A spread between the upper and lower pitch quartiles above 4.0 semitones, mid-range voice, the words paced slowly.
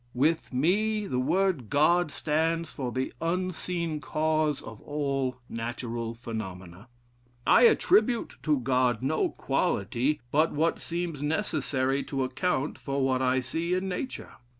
Yes: average, 4.7 semitones; medium, 145 Hz; slow, 130 wpm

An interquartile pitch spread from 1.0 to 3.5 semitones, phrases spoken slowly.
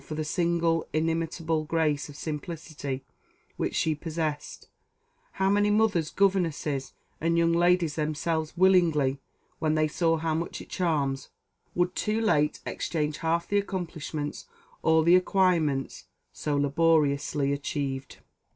Yes: narrow, 2.4 semitones; slow, 125 wpm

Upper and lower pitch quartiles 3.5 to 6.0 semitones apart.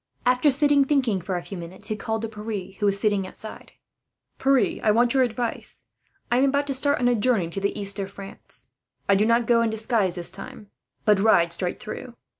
Yes: average, 4.0 semitones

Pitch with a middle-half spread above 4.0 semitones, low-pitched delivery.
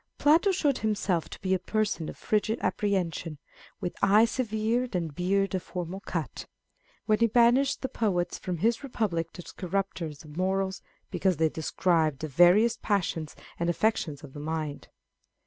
No: average, 4.7 semitones; high, 190 Hz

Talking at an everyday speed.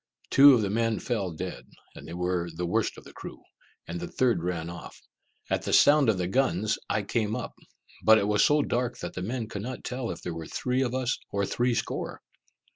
No: fast, 225 wpm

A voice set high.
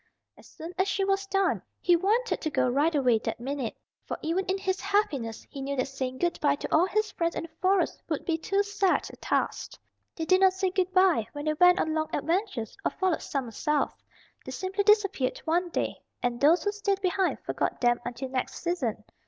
Yes: very high, 345 Hz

